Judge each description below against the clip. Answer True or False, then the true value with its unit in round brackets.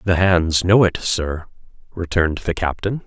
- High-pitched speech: False (90 Hz)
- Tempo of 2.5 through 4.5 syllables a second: True (4.4 syllables/s)